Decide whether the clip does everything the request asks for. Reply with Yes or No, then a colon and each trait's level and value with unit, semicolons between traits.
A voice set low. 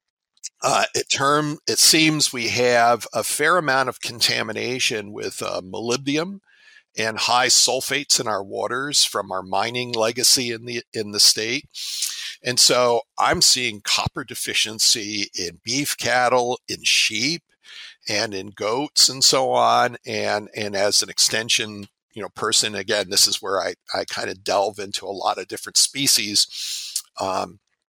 Yes: low, 120 Hz